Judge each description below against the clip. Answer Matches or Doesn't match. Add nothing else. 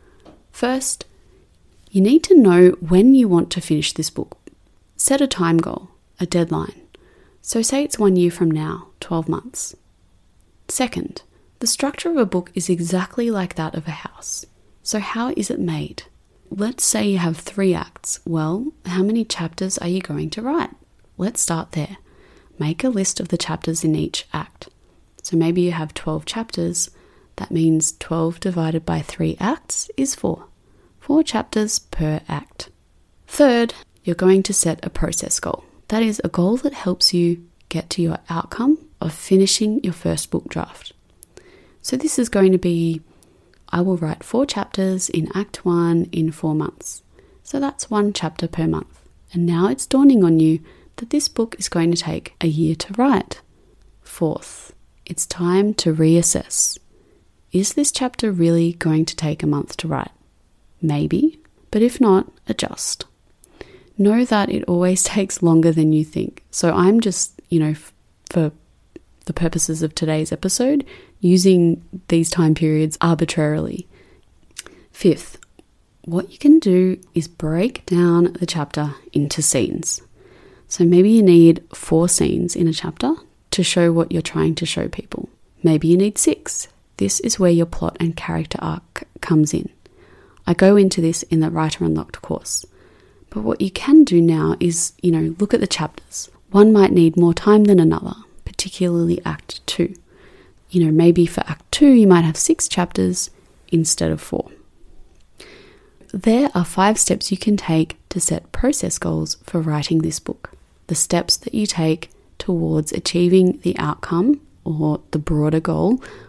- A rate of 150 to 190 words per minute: Matches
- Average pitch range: Matches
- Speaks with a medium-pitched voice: Matches